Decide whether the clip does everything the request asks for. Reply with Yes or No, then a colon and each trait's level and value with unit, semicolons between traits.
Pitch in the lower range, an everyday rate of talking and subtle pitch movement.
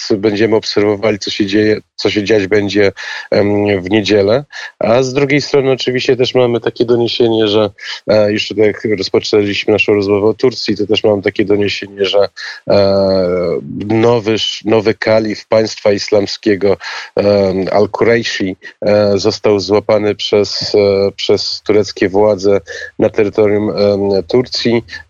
Yes: low, 105 Hz; average, 135 wpm; narrow, 1.6 semitones